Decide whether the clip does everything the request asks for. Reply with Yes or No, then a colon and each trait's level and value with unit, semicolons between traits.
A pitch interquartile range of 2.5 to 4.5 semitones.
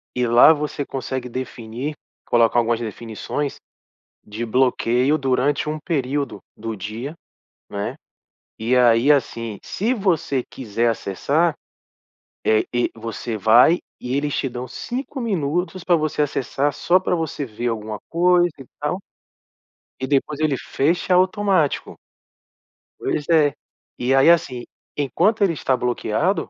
No: average, 5.1 semitones